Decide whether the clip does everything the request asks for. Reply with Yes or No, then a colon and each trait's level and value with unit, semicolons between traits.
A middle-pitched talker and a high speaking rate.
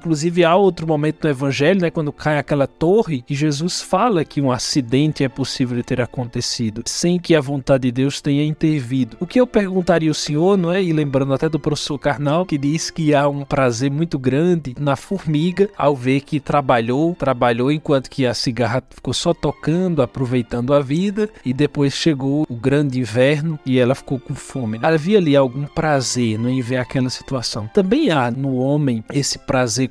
Yes: medium, 145 Hz; fast, 195 wpm